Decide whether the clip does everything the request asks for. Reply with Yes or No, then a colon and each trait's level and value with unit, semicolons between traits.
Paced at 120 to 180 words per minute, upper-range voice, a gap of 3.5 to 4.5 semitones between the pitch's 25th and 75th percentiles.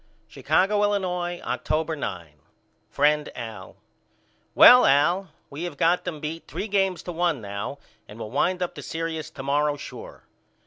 No: average, 150 wpm; medium, 160 Hz; average, 4.1 semitones